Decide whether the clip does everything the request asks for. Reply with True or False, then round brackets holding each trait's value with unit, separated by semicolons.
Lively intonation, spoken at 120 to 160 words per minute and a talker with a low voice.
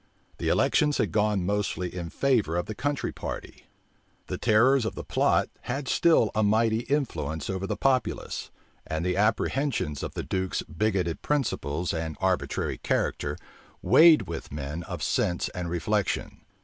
True (6.2 semitones; 150 wpm; 100 Hz)